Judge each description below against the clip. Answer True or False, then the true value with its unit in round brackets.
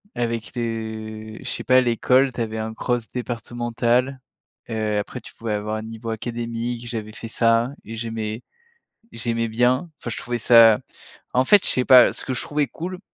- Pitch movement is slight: True (1.7 semitones)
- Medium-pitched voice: False (115 Hz)